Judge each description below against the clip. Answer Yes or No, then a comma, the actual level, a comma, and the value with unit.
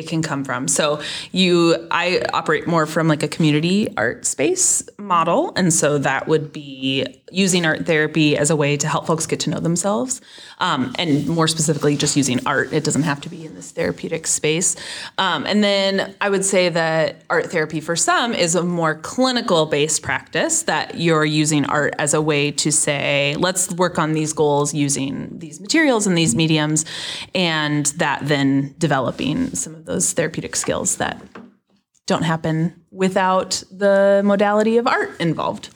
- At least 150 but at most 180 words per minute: Yes, average, 175 wpm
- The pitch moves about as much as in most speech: Yes, average, 3.6 semitones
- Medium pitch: Yes, medium, 160 Hz